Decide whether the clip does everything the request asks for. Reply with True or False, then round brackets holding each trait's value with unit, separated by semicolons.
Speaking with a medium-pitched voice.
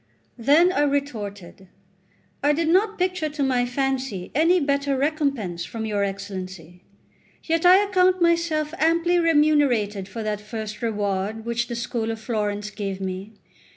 False (245 Hz)